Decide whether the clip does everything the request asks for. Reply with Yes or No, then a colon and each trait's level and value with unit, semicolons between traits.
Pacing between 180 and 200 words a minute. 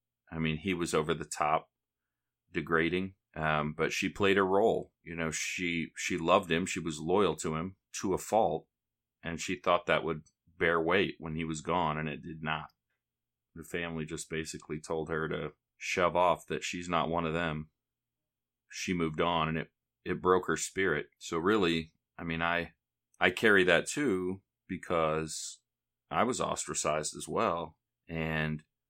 No: average, 170 wpm